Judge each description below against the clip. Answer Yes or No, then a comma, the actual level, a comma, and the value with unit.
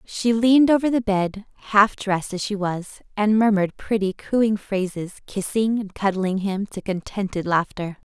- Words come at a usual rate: Yes, average, 165 wpm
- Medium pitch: No, high, 205 Hz